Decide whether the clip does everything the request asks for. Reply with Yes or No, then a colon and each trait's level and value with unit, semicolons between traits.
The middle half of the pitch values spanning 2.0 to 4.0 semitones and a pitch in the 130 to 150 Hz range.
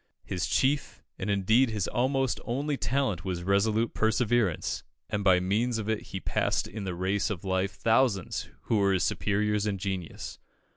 No: average, 3.4 semitones; low, 105 Hz